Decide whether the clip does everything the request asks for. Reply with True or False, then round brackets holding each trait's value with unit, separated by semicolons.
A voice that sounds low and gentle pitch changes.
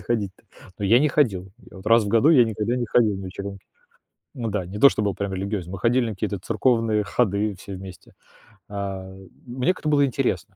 False (105 Hz; 3.7 semitones)